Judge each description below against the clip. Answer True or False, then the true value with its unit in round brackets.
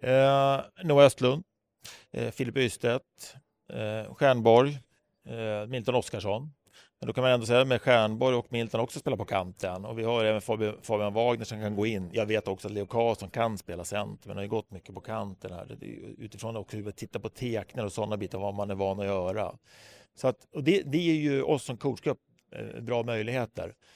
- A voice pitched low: True (115 Hz)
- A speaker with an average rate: False (210 wpm)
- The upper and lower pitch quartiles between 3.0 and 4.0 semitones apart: True (3.5 semitones)